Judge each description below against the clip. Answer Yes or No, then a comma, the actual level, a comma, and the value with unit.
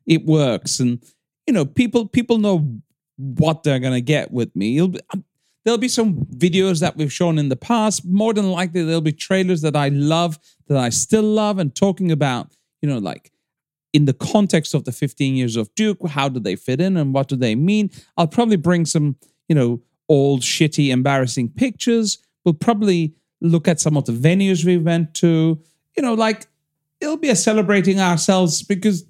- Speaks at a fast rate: No, average, 195 wpm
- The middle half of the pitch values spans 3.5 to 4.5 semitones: No, average, 5.2 semitones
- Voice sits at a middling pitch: Yes, medium, 165 Hz